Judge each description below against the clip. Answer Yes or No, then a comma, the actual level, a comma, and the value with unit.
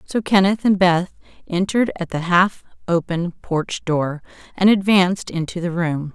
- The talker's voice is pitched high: No, medium, 180 Hz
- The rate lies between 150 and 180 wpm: Yes, average, 155 wpm